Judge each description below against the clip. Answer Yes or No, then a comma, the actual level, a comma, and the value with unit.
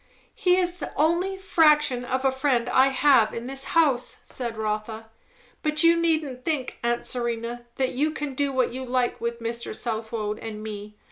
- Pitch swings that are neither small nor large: Yes, average, 4.3 semitones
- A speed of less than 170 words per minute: No, average, 180 wpm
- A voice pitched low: No, very high, 255 Hz